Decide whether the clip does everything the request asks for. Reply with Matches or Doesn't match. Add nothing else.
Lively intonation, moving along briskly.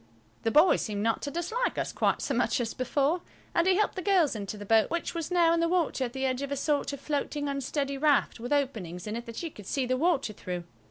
Matches